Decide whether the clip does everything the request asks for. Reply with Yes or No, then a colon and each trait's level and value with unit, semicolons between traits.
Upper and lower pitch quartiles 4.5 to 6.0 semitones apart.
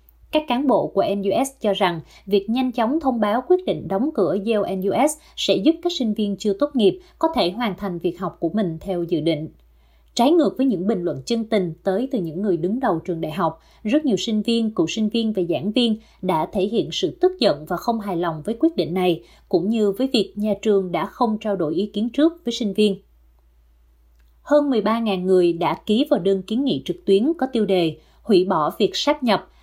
Yes: average, 5.2 semitones